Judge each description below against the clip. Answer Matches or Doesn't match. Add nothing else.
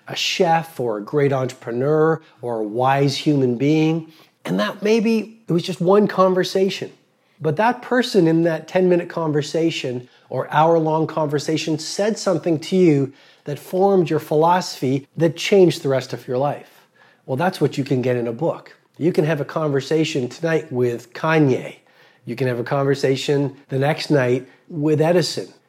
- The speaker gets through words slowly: Doesn't match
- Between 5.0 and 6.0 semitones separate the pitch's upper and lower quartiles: Doesn't match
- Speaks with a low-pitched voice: Doesn't match